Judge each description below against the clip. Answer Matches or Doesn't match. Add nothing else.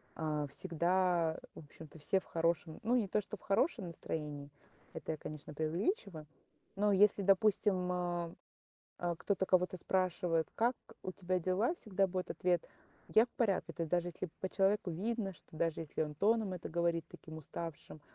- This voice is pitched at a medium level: Matches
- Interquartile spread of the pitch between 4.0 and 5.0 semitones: Doesn't match